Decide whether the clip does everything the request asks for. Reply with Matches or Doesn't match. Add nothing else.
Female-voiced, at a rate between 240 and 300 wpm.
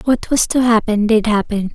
Doesn't match